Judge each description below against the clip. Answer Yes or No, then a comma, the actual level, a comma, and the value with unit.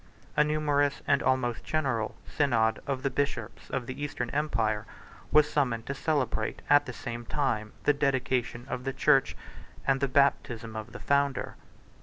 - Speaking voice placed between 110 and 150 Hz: Yes, low, 135 Hz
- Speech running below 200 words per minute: Yes, average, 160 wpm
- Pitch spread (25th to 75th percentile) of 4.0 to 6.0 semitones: No, average, 3.2 semitones